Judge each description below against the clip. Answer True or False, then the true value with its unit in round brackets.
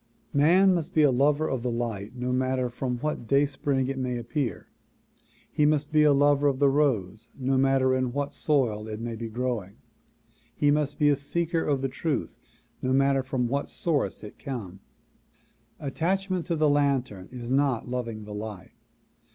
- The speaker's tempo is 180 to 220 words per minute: True (185 wpm)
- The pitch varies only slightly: False (3.2 semitones)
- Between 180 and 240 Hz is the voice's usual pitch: False (135 Hz)